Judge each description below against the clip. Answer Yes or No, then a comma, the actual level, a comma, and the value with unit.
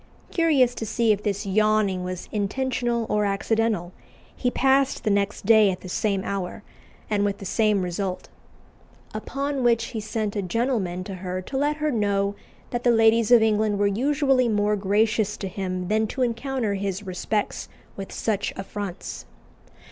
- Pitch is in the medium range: No, high, 210 Hz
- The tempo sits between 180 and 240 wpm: No, average, 165 wpm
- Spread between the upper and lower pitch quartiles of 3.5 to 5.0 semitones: No, average, 3.0 semitones